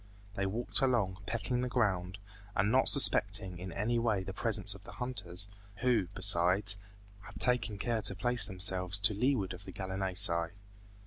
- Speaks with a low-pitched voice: Yes, low, 100 Hz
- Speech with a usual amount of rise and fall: Yes, average, 3.9 semitones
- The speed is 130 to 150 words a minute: No, average, 165 wpm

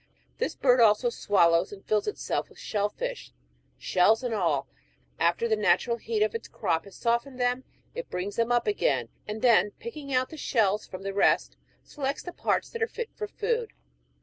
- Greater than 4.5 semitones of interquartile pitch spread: Yes, wide, 5.4 semitones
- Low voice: No, high, 235 Hz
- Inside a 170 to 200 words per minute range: Yes, average, 190 wpm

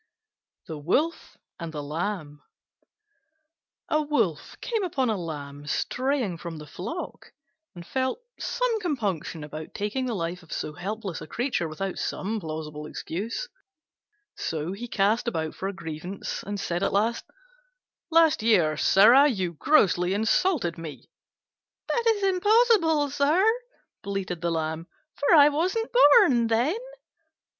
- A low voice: No, high, 205 Hz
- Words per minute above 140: No, slow, 135 wpm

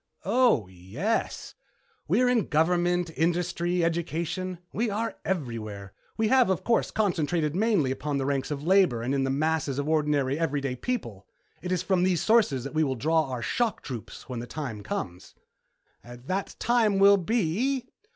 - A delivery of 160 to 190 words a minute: Yes, average, 165 wpm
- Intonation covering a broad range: Yes, wide, 6.6 semitones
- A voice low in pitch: No, medium, 160 Hz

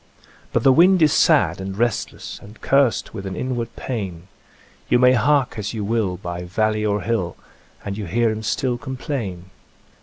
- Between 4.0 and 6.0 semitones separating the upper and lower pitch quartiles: Yes, average, 4.5 semitones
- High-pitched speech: No, low, 110 Hz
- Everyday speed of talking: Yes, average, 175 wpm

